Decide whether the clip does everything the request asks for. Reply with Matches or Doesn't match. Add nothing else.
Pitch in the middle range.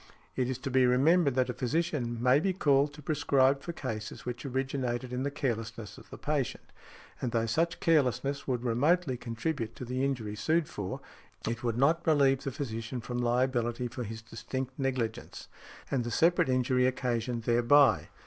Doesn't match